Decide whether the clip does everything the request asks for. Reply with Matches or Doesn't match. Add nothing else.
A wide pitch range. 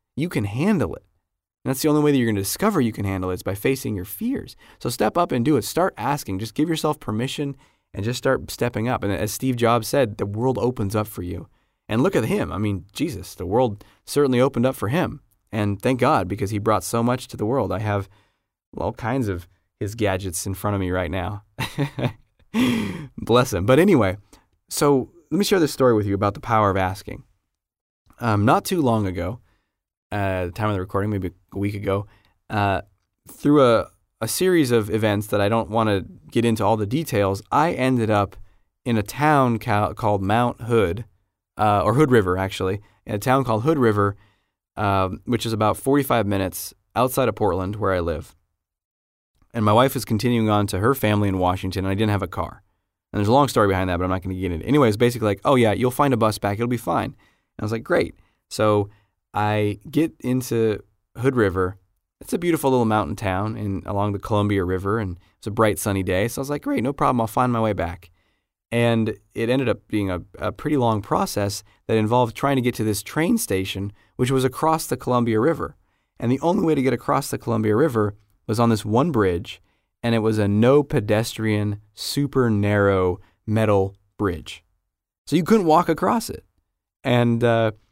Doesn't match